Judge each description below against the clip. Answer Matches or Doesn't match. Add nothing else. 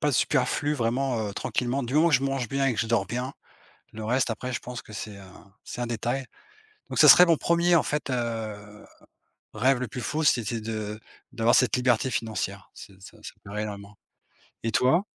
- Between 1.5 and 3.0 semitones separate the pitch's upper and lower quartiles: Doesn't match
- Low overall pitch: Matches